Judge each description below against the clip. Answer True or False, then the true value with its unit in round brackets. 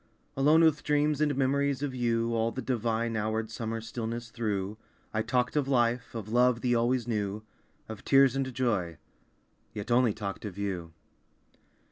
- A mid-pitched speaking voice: False (115 Hz)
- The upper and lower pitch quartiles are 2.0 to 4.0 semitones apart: True (3.0 semitones)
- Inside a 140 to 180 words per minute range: True (160 wpm)